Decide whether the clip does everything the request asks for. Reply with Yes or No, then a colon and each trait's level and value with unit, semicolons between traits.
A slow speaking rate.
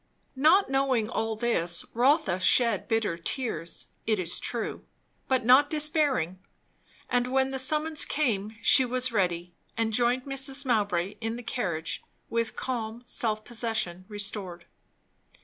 Yes: slow, 130 wpm